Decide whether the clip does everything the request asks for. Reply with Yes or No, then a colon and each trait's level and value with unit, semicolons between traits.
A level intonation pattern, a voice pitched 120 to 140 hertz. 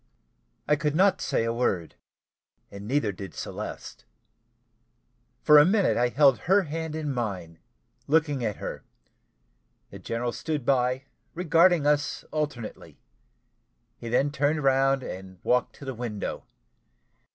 No: average, 4.3 semitones; low, 135 Hz